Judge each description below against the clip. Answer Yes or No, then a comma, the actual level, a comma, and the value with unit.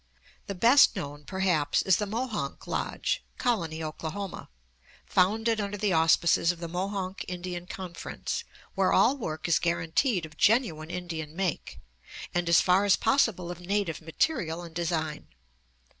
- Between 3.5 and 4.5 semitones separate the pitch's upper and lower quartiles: Yes, average, 3.8 semitones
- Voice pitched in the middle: Yes, medium, 180 Hz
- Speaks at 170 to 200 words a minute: No, average, 145 wpm